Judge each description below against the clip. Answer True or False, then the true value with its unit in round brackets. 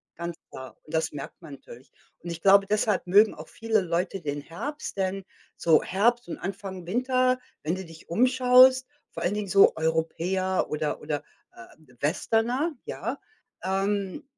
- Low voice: False (190 Hz)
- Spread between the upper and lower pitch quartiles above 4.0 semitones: True (5.4 semitones)